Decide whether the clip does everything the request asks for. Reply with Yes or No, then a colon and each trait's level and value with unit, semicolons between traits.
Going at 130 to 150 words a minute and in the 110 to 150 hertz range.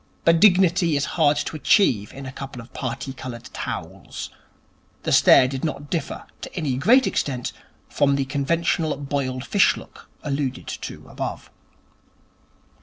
Yes: average, 145 wpm; medium, 140 Hz